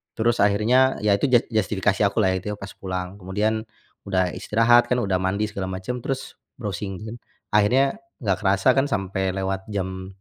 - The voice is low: Yes, low, 100 Hz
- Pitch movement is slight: No, average, 3.1 semitones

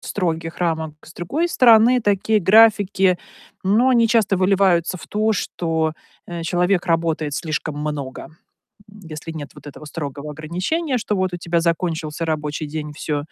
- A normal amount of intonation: Yes, average, 4.5 semitones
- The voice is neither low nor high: Yes, medium, 170 Hz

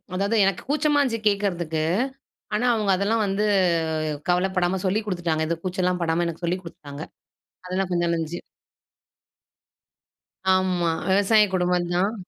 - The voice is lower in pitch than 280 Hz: Yes, medium, 185 Hz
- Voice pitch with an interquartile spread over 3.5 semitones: No, average, 2.7 semitones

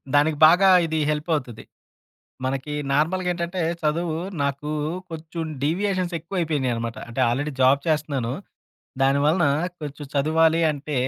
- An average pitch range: Yes, average, 3.1 semitones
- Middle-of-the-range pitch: Yes, medium, 155 Hz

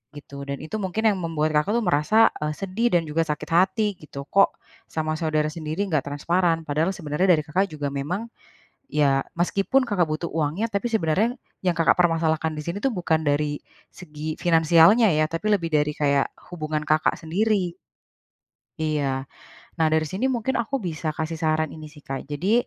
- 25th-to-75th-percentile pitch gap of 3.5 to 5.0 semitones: Yes, average, 3.8 semitones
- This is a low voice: No, medium, 160 Hz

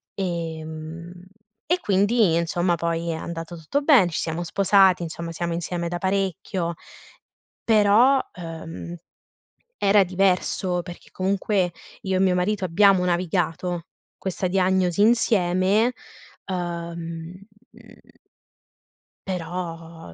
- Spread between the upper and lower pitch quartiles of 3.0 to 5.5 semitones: No, narrow, 2.5 semitones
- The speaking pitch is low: No, medium, 180 Hz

